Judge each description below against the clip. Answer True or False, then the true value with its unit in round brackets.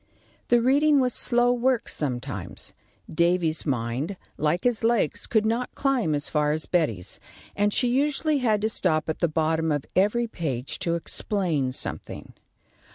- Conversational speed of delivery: True (155 wpm)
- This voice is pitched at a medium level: True (180 Hz)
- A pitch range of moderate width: False (7.6 semitones)